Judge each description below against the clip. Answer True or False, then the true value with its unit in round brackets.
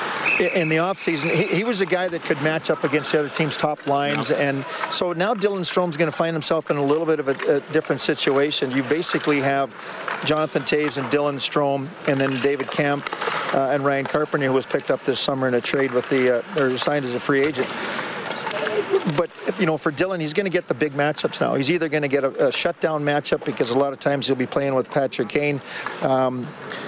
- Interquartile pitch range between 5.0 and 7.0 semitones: False (3.0 semitones)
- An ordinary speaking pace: False (230 wpm)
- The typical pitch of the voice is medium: True (150 Hz)